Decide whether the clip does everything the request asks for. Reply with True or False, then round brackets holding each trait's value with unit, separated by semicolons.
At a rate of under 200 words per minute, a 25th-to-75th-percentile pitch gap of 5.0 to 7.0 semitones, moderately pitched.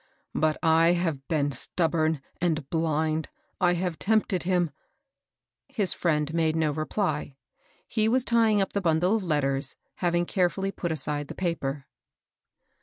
False (150 wpm; 3.0 semitones; 165 Hz)